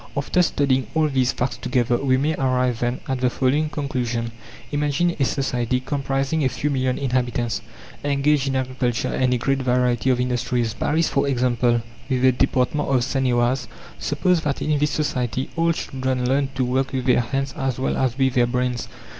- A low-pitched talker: Yes, low, 130 Hz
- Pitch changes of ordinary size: No, narrow, 1.9 semitones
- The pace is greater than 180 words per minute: Yes, average, 190 wpm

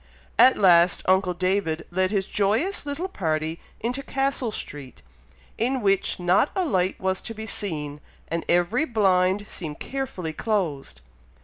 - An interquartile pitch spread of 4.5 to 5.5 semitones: Yes, average, 5.0 semitones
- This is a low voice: No, high, 190 Hz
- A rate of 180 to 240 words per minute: No, average, 140 wpm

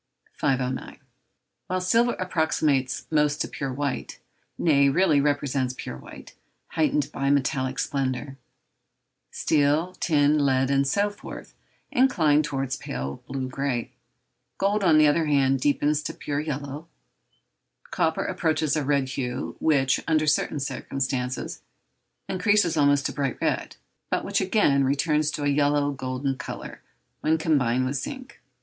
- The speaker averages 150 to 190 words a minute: No, slow, 135 wpm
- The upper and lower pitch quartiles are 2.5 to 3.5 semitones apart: Yes, average, 2.8 semitones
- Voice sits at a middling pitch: Yes, medium, 145 Hz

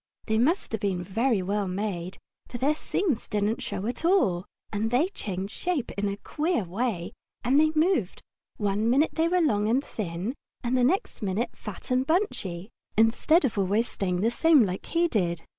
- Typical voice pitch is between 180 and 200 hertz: No, high, 225 Hz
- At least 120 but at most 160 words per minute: No, average, 185 wpm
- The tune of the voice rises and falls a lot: Yes, wide, 6.6 semitones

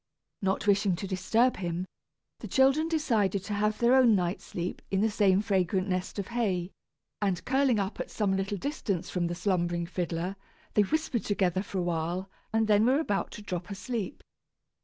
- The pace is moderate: Yes, average, 180 wpm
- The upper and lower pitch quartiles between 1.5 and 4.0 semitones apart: Yes, average, 3.4 semitones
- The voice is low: No, high, 195 Hz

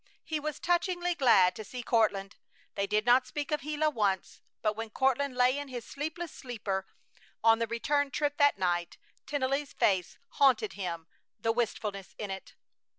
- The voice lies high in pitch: Yes, high, 245 Hz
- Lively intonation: Yes, wide, 5.9 semitones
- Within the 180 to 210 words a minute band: No, average, 165 wpm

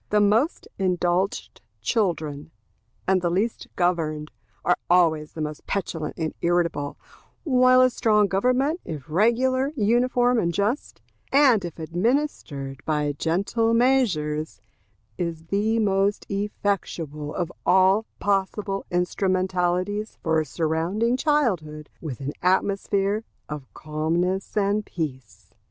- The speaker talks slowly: Yes, slow, 110 wpm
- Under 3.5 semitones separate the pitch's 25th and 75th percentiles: No, average, 5.2 semitones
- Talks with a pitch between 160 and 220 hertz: Yes, medium, 185 Hz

